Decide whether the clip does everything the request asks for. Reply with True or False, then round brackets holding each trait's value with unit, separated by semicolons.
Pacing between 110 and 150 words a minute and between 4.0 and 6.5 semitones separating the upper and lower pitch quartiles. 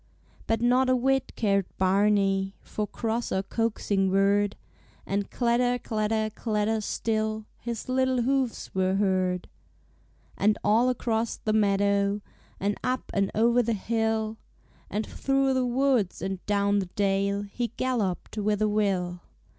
False (140 wpm; 3.0 semitones)